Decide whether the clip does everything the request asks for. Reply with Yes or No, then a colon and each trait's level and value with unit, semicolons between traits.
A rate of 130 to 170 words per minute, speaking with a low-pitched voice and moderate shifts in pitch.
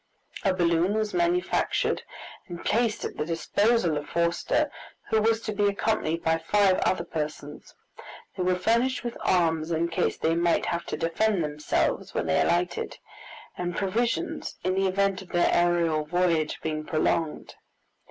No: average, 155 wpm; medium, 175 Hz; average, 3.9 semitones